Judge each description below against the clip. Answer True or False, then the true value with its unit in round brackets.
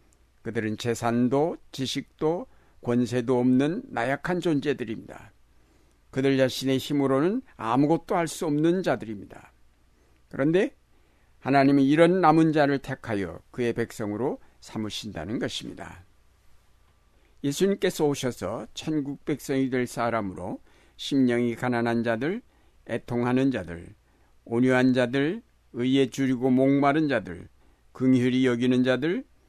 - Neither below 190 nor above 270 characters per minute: True (265 characters per minute)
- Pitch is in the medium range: False (125 Hz)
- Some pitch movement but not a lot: True (3.7 semitones)